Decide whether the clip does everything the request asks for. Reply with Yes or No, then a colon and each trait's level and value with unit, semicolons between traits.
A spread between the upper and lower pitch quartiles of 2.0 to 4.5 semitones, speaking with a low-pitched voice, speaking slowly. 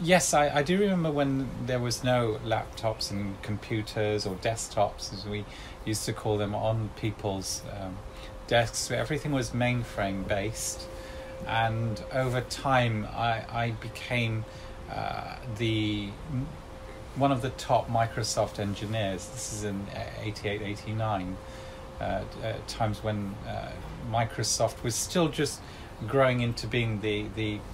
Yes: narrow, 2.6 semitones; low, 110 Hz; slow, 130 wpm